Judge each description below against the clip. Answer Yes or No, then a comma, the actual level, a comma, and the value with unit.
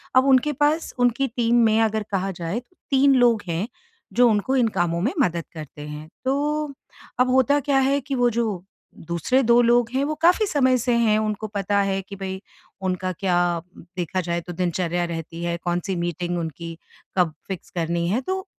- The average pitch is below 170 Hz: No, high, 205 Hz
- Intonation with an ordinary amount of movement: No, wide, 6.5 semitones